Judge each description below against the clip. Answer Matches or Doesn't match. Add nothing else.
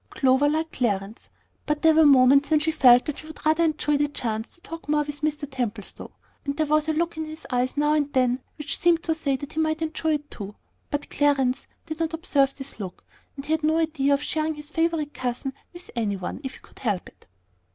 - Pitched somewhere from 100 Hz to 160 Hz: Doesn't match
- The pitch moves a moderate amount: Matches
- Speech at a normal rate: Doesn't match